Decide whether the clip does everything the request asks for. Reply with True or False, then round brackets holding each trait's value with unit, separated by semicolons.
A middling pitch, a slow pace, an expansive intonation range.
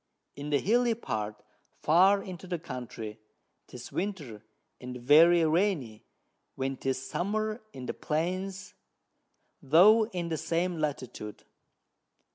True (160 Hz; 115 wpm; 6.8 semitones)